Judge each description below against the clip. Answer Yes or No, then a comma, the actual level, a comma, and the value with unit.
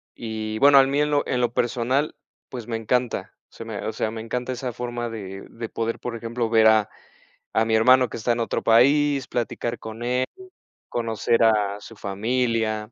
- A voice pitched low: Yes, low, 115 Hz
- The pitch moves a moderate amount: No, narrow, 2.0 semitones